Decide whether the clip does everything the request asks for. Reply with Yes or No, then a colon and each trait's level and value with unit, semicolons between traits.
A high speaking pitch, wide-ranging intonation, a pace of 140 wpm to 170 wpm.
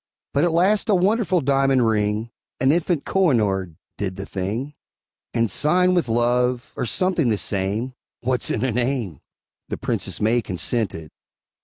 No: low, 125 Hz; wide, 6.4 semitones; average, 150 wpm